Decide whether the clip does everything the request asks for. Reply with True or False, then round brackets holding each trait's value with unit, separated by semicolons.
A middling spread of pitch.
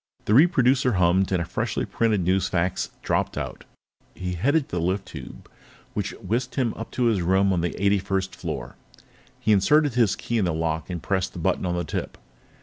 True (4.6 semitones)